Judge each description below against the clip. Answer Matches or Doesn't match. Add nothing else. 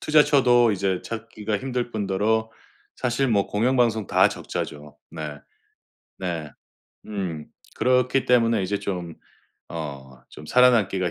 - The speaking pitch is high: Doesn't match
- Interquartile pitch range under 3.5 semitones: Doesn't match